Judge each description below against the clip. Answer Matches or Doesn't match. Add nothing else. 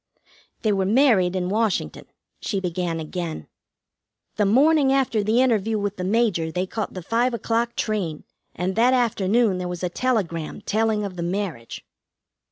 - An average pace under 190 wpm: Matches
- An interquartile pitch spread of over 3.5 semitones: Matches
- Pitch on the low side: Doesn't match